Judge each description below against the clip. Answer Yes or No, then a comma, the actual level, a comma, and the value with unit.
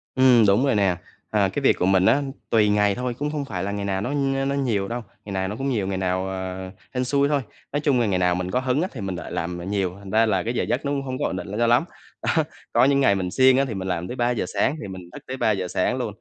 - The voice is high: No, low, 105 Hz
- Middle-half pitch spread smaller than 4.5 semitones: No, wide, 5.5 semitones